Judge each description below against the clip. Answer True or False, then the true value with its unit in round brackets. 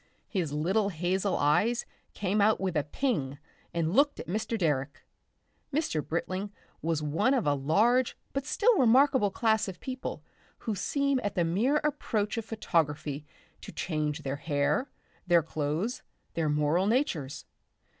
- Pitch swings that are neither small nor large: False (7.3 semitones)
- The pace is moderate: True (145 wpm)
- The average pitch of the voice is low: False (185 Hz)